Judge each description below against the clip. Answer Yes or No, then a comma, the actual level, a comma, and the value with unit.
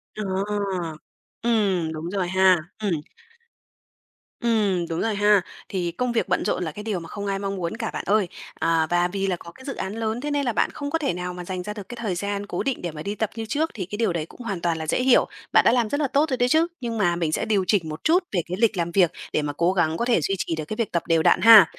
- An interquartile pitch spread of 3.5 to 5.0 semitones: Yes, average, 4.7 semitones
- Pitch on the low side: No, high, 195 Hz